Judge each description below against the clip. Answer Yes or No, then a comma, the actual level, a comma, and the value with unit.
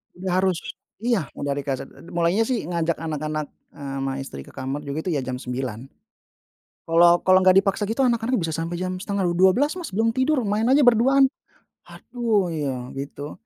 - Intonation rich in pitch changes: Yes, wide, 7.7 semitones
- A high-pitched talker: No, medium, 175 Hz